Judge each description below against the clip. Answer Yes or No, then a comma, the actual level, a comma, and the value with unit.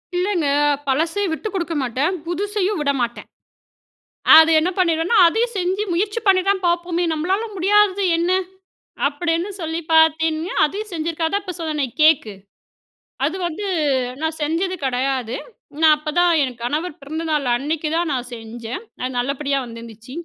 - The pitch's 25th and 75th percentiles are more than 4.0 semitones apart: Yes, average, 4.5 semitones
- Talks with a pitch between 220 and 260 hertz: No, very high, 320 Hz